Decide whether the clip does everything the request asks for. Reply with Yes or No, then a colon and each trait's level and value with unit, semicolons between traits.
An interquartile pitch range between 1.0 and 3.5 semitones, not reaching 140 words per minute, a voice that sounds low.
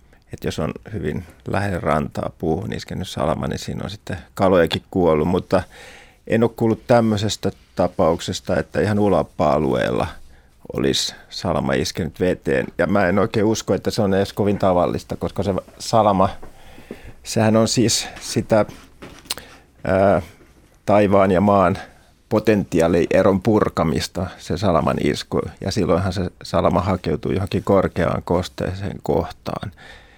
No: average, 4.5 semitones; average, 125 wpm; very low, 95 Hz